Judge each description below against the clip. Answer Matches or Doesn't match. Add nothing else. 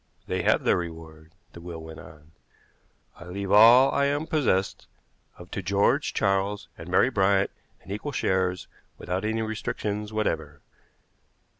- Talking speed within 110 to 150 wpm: Matches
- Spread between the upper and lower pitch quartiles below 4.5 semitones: Matches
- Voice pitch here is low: Matches